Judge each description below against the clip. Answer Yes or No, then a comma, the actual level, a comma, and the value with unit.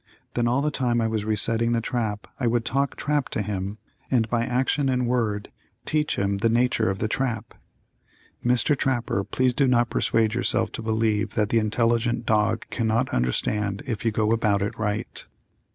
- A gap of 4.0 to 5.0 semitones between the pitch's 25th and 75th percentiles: No, narrow, 2.5 semitones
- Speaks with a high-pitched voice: No, low, 115 Hz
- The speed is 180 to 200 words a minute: Yes, average, 185 wpm